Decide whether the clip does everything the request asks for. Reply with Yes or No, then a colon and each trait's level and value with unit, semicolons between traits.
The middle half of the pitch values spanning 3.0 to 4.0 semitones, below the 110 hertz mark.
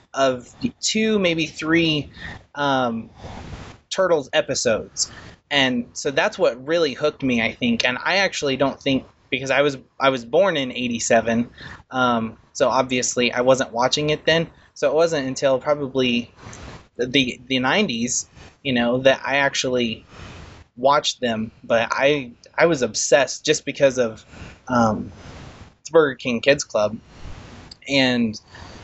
No: average, 3.3 semitones; low, 130 Hz